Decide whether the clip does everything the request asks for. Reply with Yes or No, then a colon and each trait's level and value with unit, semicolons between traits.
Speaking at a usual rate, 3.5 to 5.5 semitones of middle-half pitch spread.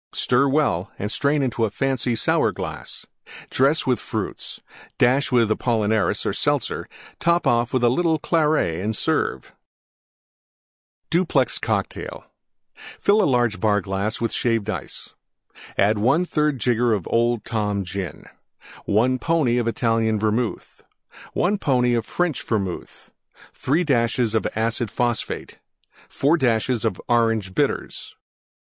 No: slow, 115 wpm; average, 3.9 semitones